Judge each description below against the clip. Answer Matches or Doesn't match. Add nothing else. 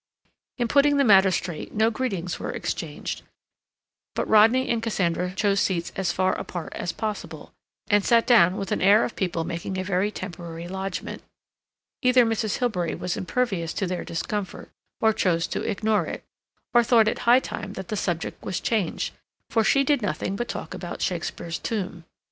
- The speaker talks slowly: Doesn't match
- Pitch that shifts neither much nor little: Matches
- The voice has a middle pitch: Doesn't match